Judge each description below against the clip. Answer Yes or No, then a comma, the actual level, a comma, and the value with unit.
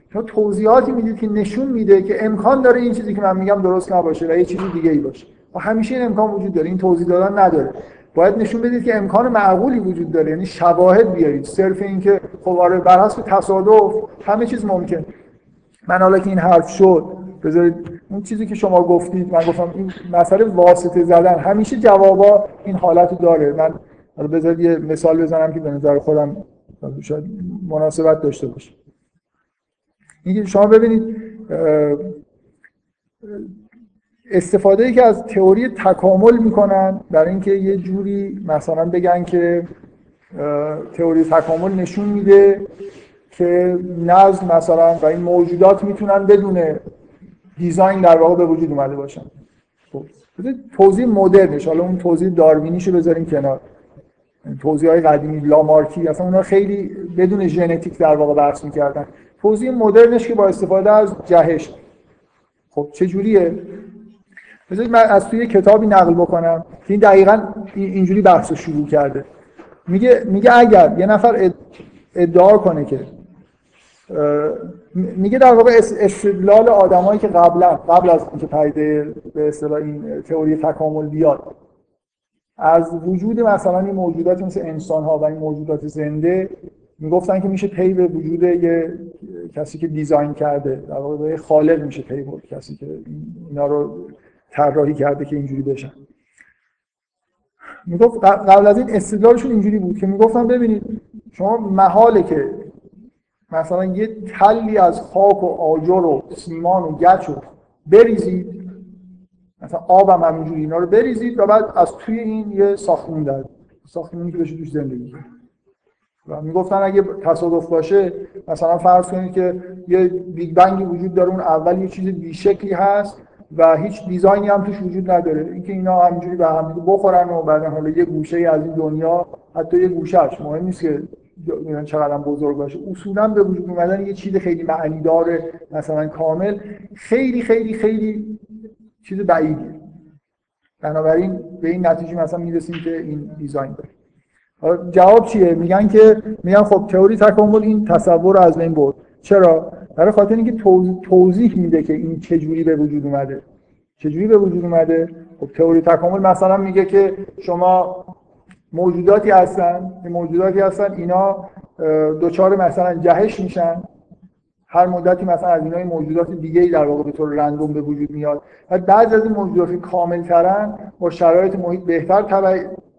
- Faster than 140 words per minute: Yes, average, 150 wpm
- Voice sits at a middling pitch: Yes, medium, 180 Hz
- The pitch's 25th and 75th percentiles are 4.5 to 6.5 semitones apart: No, average, 3.5 semitones